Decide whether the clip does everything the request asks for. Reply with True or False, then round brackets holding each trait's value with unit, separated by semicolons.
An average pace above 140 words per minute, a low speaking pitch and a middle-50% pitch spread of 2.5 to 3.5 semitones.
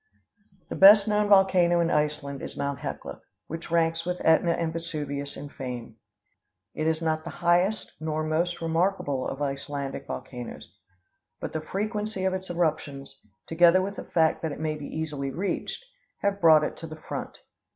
False (170 wpm; 160 Hz; 3.2 semitones)